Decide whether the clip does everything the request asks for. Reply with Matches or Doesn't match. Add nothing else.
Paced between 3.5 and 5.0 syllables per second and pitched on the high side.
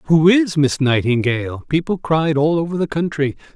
Doesn't match